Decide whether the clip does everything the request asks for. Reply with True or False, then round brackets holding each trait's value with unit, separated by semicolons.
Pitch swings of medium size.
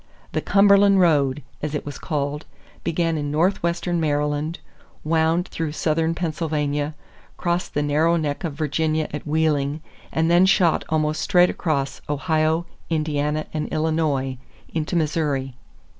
False (2.0 semitones)